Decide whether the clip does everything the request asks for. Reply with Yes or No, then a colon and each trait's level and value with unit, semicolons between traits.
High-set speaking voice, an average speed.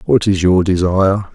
No: very low, 95 Hz; average, 180 wpm